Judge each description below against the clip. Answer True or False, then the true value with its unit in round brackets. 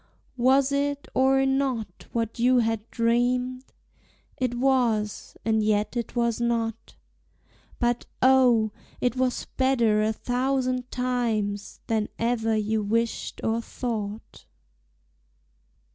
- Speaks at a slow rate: True (110 wpm)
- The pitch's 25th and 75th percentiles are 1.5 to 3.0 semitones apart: True (2.5 semitones)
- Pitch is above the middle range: True (235 Hz)